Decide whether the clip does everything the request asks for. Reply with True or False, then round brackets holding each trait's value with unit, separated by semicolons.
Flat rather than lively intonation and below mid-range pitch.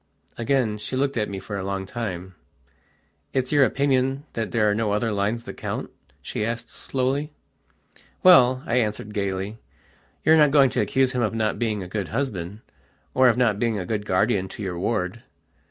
False (4.1 semitones; 115 Hz)